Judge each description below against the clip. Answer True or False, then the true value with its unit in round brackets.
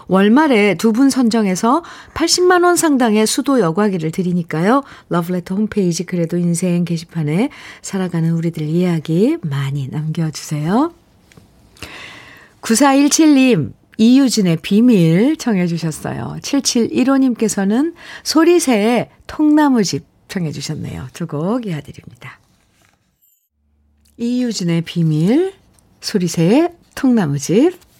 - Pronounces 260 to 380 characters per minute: False (240 characters per minute)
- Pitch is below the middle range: False (205 Hz)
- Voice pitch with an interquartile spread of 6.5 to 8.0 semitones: True (7.7 semitones)